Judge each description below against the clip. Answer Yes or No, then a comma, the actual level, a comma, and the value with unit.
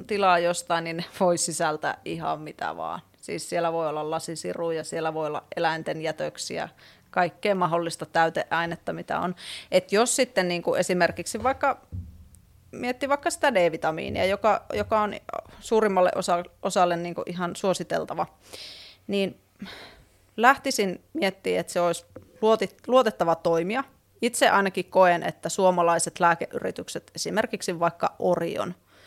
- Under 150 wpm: Yes, average, 125 wpm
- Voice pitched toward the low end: No, medium, 175 Hz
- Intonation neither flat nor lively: Yes, average, 3.7 semitones